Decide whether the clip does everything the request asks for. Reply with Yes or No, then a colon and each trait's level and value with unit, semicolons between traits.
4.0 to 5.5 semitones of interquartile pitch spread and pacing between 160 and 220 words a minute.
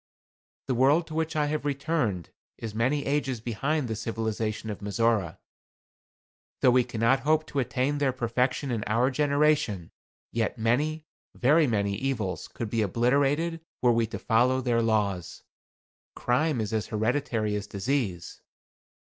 No: average, 4.5 semitones; average, 145 wpm